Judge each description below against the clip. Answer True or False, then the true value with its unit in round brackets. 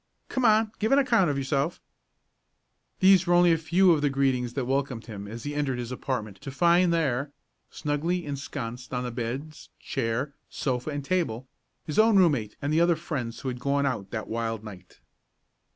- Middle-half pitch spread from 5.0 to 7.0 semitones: True (5.6 semitones)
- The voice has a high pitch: False (140 Hz)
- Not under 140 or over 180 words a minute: False (190 wpm)